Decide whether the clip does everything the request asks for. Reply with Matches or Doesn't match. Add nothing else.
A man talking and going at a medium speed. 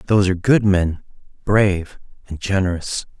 Doesn't match